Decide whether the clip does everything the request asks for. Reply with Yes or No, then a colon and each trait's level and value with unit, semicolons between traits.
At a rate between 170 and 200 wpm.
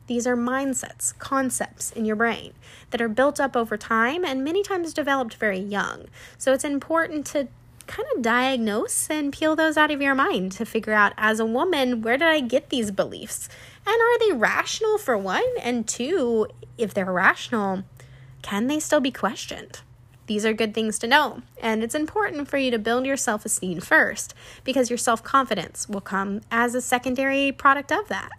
Yes: average, 190 wpm